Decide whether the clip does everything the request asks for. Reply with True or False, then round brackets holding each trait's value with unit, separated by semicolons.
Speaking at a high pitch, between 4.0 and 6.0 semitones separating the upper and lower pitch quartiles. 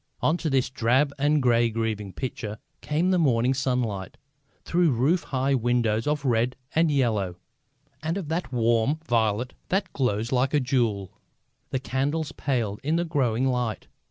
False (130 Hz; 4.4 semitones)